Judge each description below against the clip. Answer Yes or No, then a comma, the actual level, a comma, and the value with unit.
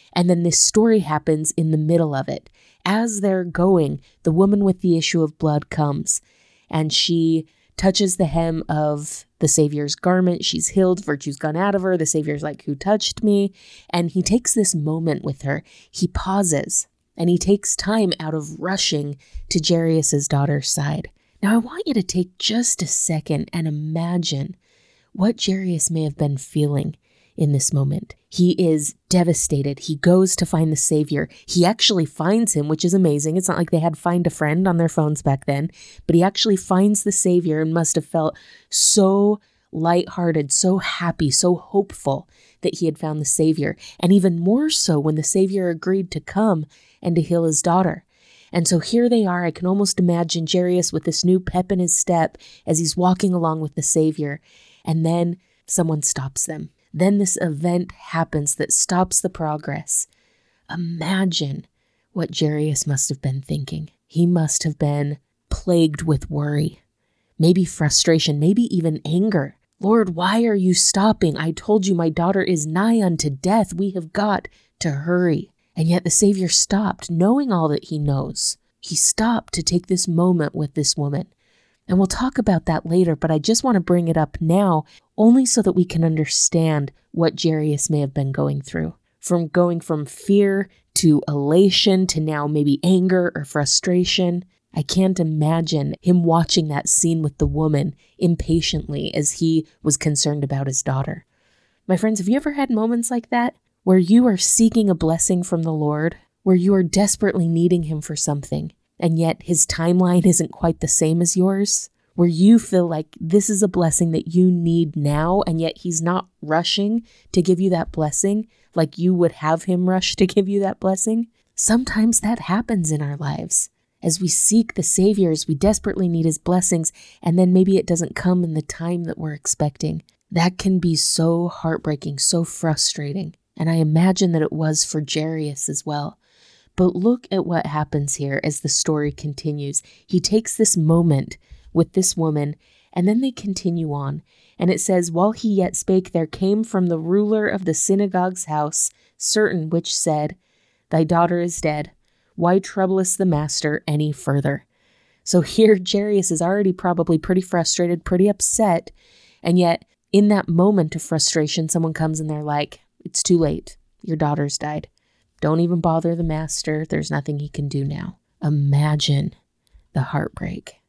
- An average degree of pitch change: Yes, average, 3.5 semitones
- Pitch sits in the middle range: Yes, medium, 170 Hz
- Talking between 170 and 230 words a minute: Yes, average, 180 wpm